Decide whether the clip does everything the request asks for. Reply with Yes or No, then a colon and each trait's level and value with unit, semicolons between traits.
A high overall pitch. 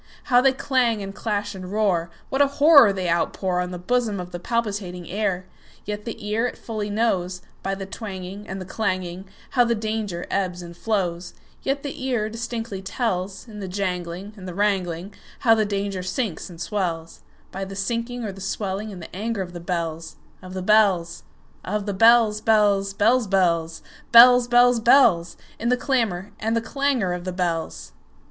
Yes: high, 200 Hz